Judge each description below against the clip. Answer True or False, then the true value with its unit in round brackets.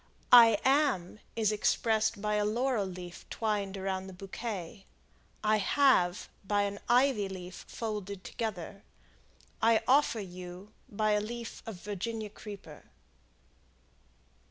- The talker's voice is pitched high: True (210 Hz)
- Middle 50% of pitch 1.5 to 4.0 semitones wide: True (2.9 semitones)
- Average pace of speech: False (120 wpm)